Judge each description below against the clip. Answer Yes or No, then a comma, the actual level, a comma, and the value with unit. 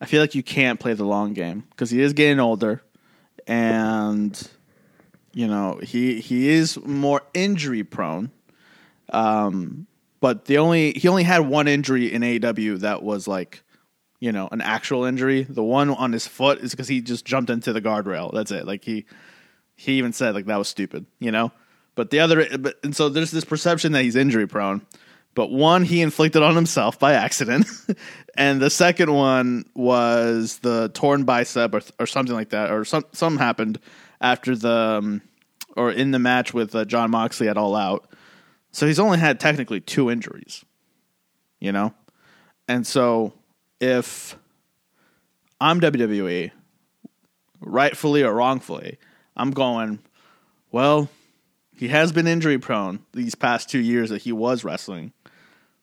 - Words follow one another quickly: No, average, 165 wpm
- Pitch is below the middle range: Yes, low, 125 Hz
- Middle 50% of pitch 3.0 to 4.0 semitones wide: No, average, 4.4 semitones